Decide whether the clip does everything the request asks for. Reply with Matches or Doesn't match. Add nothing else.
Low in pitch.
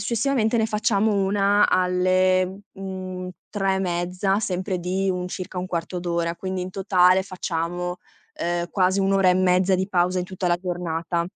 Doesn't match